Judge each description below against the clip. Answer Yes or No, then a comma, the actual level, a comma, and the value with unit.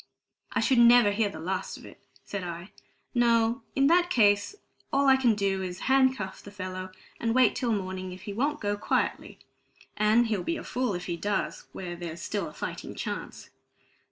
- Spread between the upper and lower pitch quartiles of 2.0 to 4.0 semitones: No, average, 4.7 semitones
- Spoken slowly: No, average, 190 wpm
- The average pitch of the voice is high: Yes, high, 205 Hz